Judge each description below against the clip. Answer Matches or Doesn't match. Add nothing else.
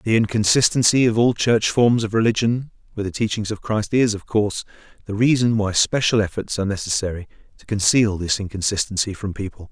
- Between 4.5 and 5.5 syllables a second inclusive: Doesn't match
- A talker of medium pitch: Doesn't match